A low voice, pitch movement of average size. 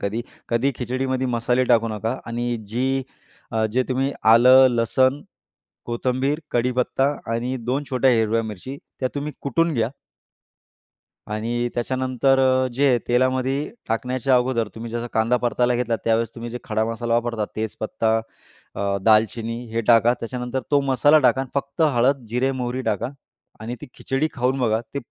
No: low, 125 Hz; narrow, 2.2 semitones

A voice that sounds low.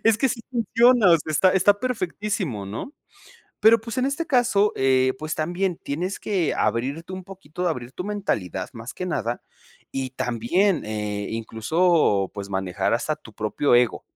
No: medium, 160 Hz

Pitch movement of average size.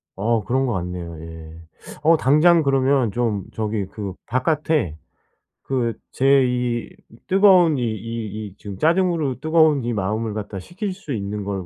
No: wide, 6.7 semitones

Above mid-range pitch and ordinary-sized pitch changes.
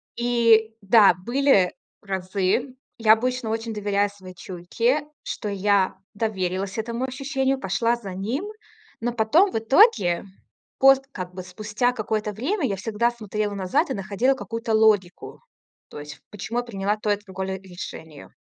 Yes: high, 215 Hz; average, 3.8 semitones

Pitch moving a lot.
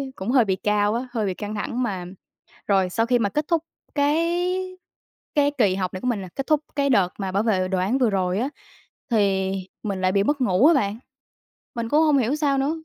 Yes: wide, 6.1 semitones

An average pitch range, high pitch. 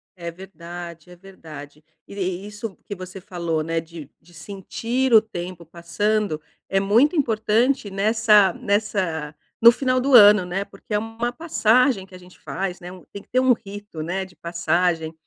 Yes: average, 4.4 semitones; high, 195 Hz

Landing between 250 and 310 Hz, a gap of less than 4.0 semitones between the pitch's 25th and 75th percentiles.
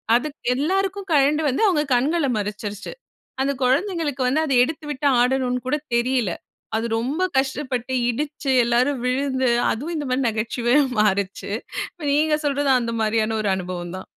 No: very high, 260 Hz; average, 4.3 semitones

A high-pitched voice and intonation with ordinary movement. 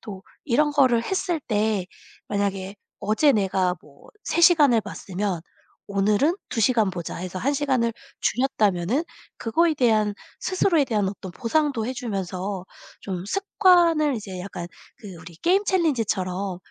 No: high, 220 Hz; wide, 7.1 semitones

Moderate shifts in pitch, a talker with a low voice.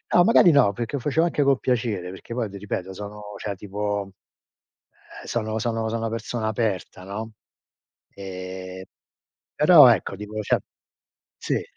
Yes: average, 3.2 semitones; low, 105 Hz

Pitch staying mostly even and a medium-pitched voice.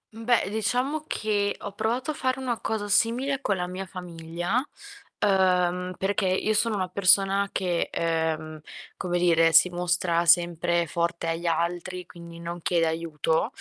No: average, 3.4 semitones; medium, 180 Hz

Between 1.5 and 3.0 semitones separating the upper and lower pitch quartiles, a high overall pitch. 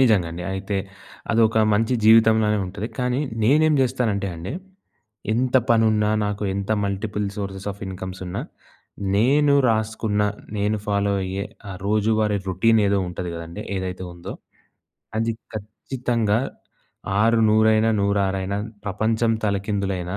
No: narrow, 2.4 semitones; low, 105 Hz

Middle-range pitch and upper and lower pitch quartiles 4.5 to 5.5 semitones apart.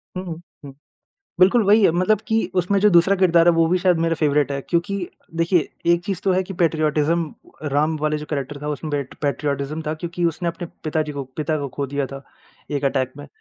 No: medium, 160 Hz; average, 3.2 semitones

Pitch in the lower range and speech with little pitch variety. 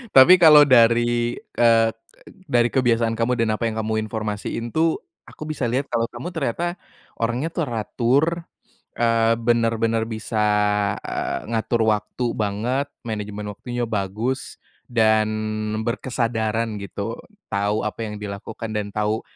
Yes: low, 115 Hz; narrow, 2.1 semitones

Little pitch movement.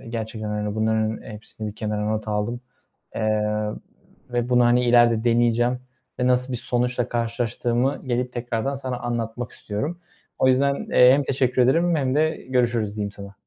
Yes: narrow, 2.3 semitones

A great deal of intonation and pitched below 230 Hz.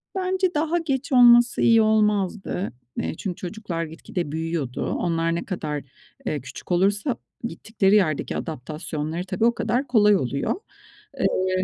Yes: wide, 6.0 semitones; high, 190 Hz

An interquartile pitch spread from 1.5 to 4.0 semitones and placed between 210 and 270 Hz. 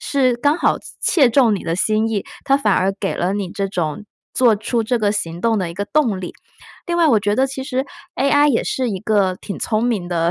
No: average, 5.1 semitones; high, 215 Hz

